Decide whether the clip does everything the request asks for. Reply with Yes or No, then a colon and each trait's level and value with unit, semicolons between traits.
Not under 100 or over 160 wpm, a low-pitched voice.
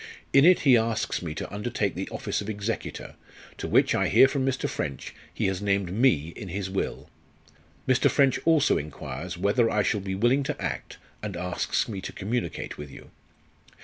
No: average, 185 wpm; low, 100 Hz